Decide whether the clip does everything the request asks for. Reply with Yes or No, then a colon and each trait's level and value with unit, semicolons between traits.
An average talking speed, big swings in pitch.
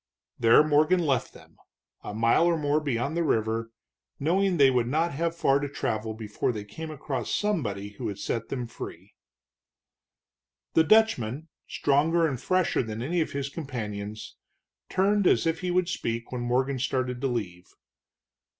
Yes: average, 160 wpm; wide, 6.1 semitones